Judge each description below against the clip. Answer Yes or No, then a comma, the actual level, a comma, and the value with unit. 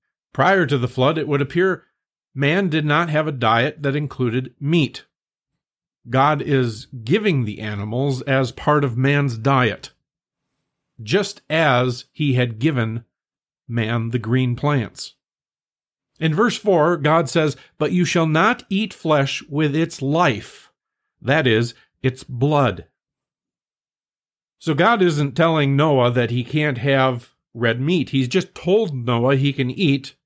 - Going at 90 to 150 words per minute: Yes, average, 140 wpm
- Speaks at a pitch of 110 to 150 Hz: Yes, medium, 140 Hz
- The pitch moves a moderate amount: Yes, average, 4.2 semitones